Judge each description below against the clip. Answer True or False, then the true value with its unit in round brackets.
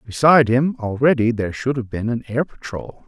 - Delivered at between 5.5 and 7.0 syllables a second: True (5.6 syllables/s)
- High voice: False (125 Hz)